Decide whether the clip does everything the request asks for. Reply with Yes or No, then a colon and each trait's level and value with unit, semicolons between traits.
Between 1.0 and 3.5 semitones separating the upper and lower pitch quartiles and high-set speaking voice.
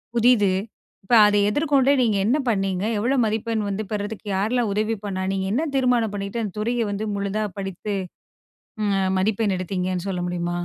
Yes: average, 3.0 semitones; high, 210 Hz